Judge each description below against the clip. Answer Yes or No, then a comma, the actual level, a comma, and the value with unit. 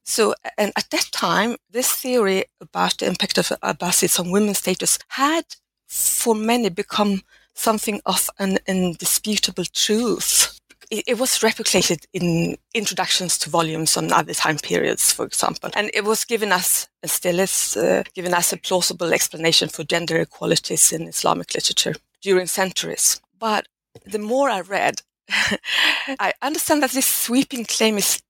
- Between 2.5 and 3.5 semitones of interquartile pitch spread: No, average, 4.0 semitones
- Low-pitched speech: No, high, 205 Hz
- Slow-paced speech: No, average, 150 wpm